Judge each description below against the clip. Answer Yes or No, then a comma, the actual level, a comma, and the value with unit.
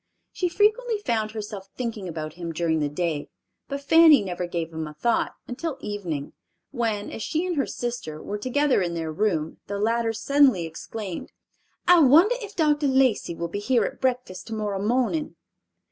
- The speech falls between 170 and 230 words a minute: Yes, average, 175 wpm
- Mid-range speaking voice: No, high, 220 Hz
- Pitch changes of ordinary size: No, wide, 8.2 semitones